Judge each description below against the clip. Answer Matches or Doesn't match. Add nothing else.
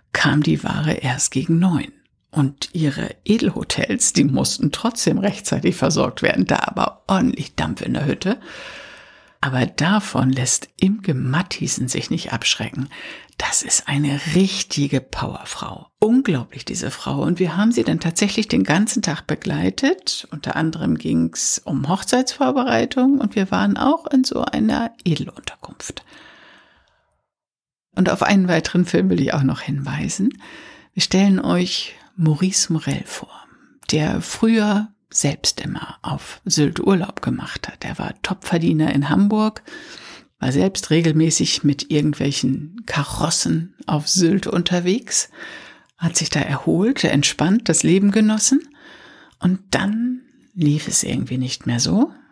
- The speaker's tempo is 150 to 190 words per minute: Doesn't match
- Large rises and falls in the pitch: Matches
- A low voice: Doesn't match